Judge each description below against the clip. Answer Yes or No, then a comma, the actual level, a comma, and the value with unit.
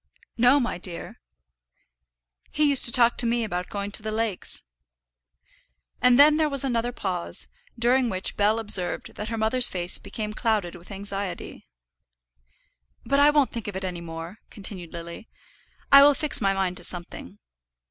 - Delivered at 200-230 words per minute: No, average, 165 wpm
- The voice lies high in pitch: Yes, high, 215 Hz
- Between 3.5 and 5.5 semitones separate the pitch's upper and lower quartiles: Yes, average, 5.0 semitones